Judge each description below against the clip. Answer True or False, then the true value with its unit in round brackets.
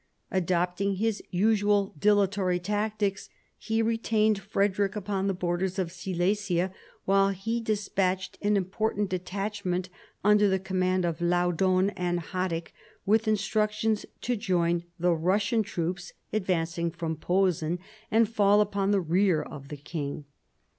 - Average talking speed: False (125 wpm)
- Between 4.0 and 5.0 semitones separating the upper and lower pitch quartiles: False (2.7 semitones)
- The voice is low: False (190 Hz)